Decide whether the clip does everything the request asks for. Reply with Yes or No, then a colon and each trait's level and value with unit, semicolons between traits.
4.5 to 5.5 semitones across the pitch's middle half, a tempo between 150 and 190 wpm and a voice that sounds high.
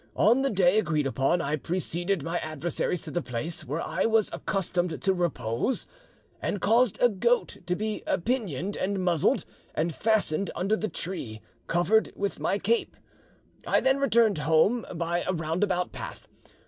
No: average, 4.9 semitones; average, 160 wpm; medium, 180 Hz